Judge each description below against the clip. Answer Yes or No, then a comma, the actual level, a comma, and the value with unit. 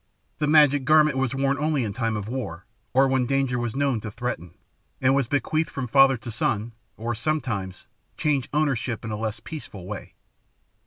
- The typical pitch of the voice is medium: No, low, 130 Hz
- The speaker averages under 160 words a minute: No, average, 180 wpm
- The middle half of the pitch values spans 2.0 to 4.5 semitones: Yes, average, 3.8 semitones